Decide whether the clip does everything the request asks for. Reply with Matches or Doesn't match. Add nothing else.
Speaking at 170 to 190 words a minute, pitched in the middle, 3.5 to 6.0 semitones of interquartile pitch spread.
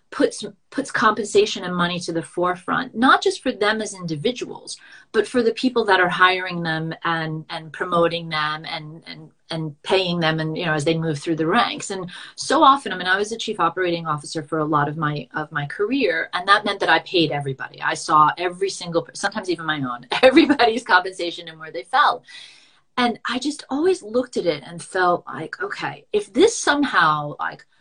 Doesn't match